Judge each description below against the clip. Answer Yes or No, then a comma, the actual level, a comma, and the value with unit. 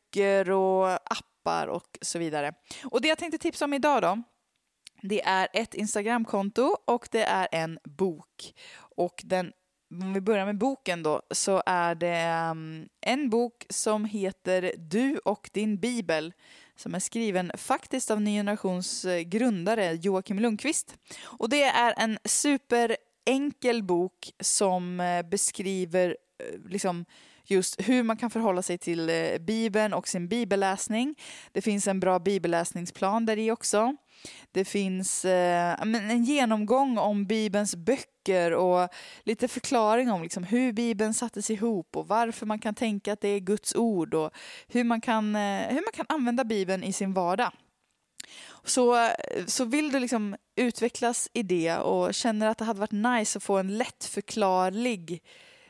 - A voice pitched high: Yes, high, 210 Hz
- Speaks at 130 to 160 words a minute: Yes, average, 150 wpm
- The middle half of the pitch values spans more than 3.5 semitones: Yes, average, 4.2 semitones